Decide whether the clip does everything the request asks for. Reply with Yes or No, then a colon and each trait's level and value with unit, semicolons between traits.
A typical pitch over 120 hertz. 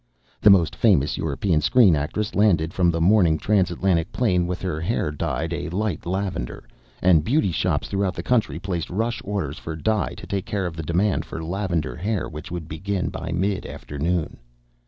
No: very low, 90 Hz